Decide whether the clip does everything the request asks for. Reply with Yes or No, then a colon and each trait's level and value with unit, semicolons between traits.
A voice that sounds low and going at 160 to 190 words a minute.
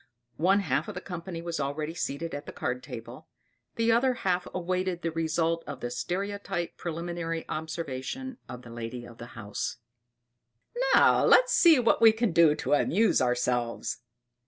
No: medium, 165 Hz; average, 165 wpm